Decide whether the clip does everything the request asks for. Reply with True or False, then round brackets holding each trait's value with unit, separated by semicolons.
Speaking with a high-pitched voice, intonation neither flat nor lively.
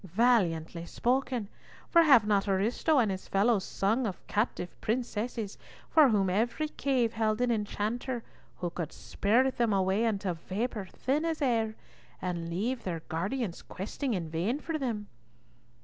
True (220 Hz; 4.5 semitones)